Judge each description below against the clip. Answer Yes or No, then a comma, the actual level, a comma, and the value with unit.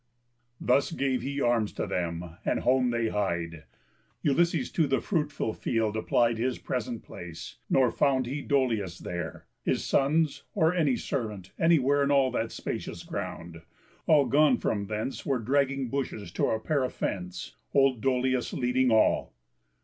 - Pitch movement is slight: No, average, 4.4 semitones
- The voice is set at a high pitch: No, low, 125 Hz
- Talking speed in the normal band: Yes, average, 150 wpm